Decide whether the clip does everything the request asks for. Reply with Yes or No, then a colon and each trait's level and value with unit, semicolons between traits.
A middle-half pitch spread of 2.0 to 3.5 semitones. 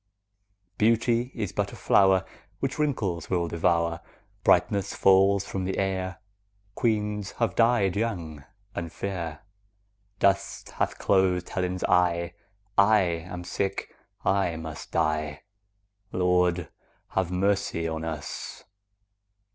Yes: average, 2.8 semitones